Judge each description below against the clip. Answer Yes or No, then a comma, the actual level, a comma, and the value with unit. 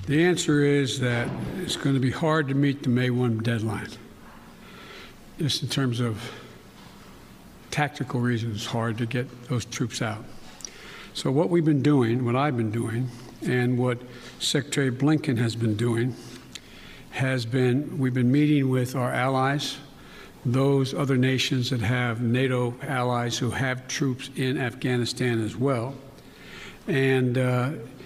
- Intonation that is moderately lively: No, narrow, 2.2 semitones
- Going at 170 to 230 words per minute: No, average, 145 wpm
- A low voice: Yes, low, 125 Hz